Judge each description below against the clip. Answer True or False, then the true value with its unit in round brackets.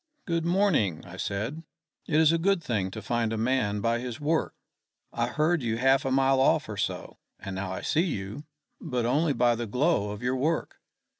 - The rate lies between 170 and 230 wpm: True (205 wpm)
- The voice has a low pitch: True (125 Hz)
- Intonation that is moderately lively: False (6.0 semitones)